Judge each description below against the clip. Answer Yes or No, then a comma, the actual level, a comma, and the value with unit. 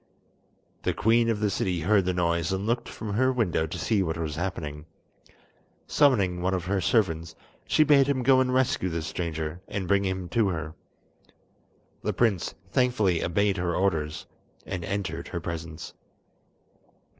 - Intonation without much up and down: No, average, 4.6 semitones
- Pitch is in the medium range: No, very low, 95 Hz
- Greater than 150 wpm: Yes, average, 160 wpm